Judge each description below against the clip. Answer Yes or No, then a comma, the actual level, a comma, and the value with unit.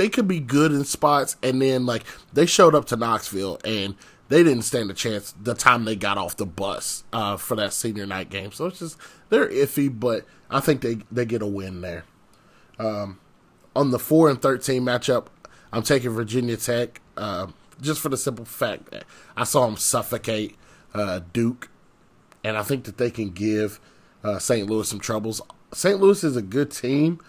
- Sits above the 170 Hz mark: No, low, 120 Hz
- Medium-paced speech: Yes, average, 195 wpm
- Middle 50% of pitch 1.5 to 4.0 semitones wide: No, average, 4.9 semitones